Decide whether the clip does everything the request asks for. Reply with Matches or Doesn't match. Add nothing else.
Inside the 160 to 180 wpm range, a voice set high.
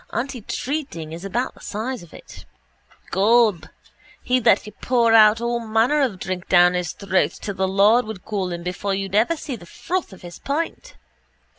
Matches